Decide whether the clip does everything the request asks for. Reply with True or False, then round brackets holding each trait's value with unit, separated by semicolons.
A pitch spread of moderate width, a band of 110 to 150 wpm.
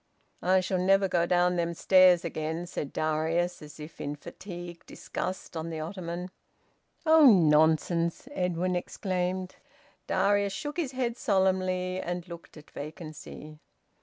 False (2.3 semitones; 135 wpm)